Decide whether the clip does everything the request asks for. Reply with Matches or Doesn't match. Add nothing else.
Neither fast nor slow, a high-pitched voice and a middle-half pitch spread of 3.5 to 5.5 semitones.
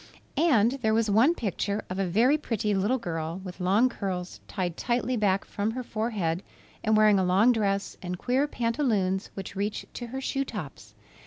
Matches